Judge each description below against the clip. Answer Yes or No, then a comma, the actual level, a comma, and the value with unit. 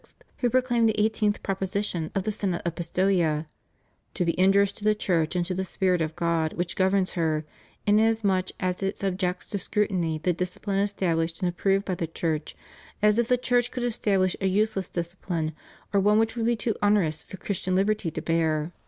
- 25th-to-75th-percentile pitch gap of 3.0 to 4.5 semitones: Yes, average, 3.5 semitones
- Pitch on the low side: No, high, 190 Hz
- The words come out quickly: No, average, 190 wpm